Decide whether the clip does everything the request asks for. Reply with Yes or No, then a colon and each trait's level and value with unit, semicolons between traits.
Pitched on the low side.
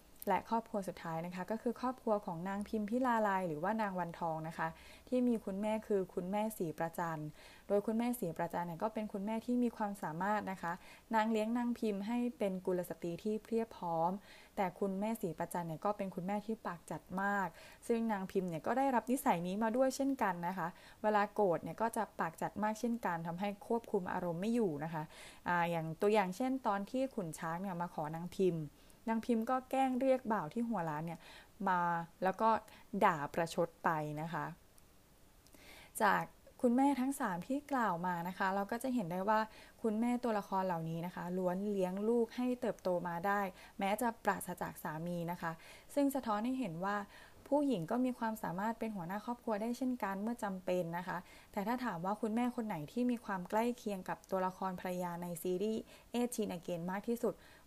No: high, 205 Hz